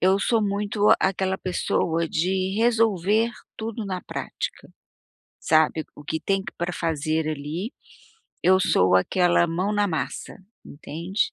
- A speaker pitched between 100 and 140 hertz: No, medium, 185 Hz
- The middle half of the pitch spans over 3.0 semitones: Yes, average, 4.0 semitones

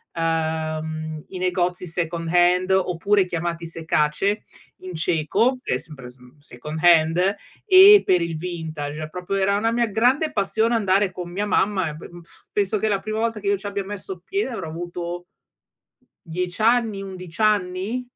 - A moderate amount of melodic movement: Yes, average, 3.9 semitones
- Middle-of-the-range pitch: Yes, medium, 180 Hz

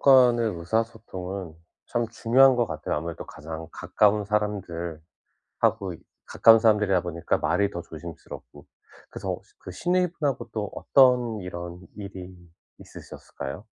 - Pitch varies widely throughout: No, average, 5.0 semitones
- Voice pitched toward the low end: Yes, low, 100 Hz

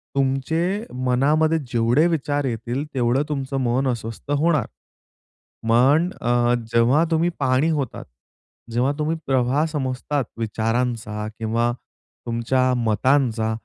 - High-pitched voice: No, low, 130 Hz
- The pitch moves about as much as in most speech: Yes, average, 3.6 semitones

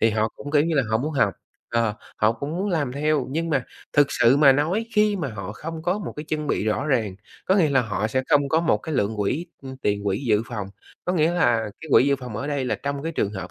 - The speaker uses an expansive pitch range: Yes, wide, 6.0 semitones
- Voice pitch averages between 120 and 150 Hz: Yes, medium, 140 Hz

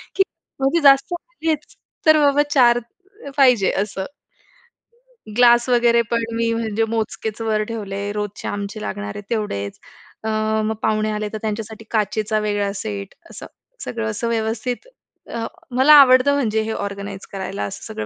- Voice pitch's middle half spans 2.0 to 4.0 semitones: Yes, average, 2.9 semitones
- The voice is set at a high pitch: Yes, high, 220 Hz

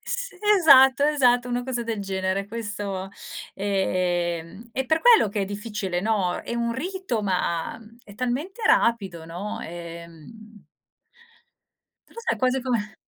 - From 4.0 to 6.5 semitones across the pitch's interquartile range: Yes, average, 5.1 semitones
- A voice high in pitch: Yes, high, 215 Hz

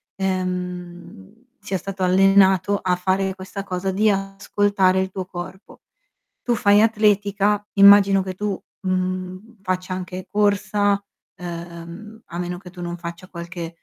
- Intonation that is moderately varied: No, narrow, 2.0 semitones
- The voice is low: No, high, 190 Hz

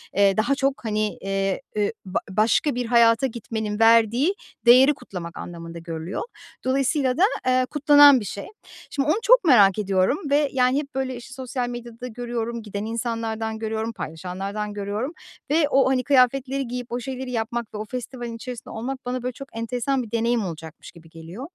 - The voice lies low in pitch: No, high, 235 Hz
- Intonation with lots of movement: No, average, 3.7 semitones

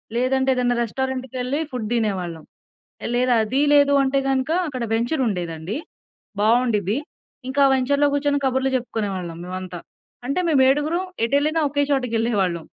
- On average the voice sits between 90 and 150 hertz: No, very high, 250 Hz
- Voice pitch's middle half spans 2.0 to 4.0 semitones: No, average, 4.5 semitones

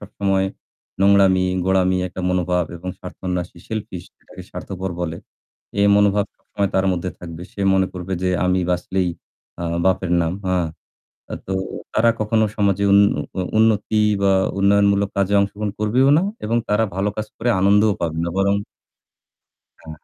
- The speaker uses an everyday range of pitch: No, narrow, 1.9 semitones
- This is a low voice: Yes, very low, 95 Hz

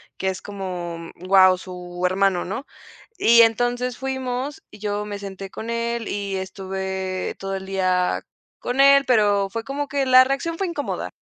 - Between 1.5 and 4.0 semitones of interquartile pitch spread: No, average, 4.8 semitones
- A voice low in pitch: No, high, 205 Hz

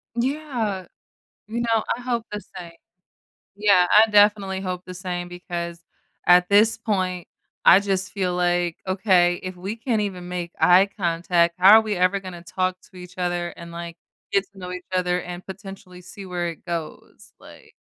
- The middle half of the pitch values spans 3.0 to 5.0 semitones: No, narrow, 2.4 semitones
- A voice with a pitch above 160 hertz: Yes, medium, 185 Hz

